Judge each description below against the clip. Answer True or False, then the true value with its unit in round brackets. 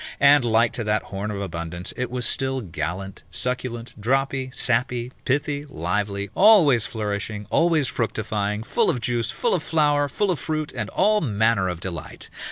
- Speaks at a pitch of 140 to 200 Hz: False (120 Hz)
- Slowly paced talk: False (165 wpm)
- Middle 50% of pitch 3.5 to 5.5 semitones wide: True (5.1 semitones)